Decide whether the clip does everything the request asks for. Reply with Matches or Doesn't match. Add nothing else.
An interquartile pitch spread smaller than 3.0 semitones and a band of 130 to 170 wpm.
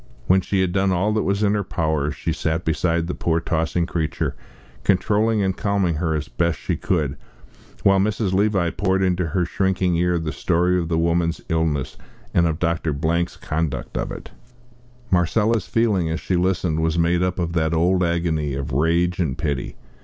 Doesn't match